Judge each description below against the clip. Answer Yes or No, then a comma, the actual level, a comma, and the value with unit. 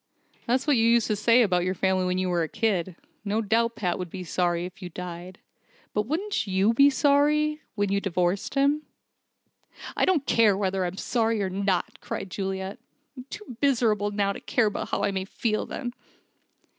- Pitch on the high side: Yes, high, 205 Hz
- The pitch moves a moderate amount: Yes, average, 4.3 semitones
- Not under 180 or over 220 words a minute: Yes, average, 195 wpm